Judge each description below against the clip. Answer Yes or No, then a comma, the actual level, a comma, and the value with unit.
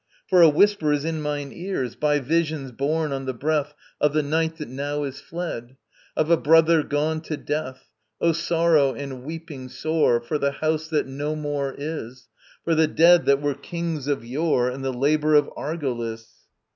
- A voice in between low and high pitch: Yes, medium, 150 Hz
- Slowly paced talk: No, average, 185 wpm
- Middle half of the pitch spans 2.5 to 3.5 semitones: Yes, average, 2.8 semitones